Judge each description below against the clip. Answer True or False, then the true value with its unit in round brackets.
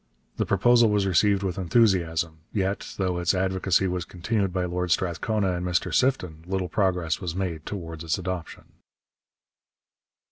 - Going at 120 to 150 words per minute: True (145 wpm)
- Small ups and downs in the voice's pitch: True (2.0 semitones)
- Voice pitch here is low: True (90 Hz)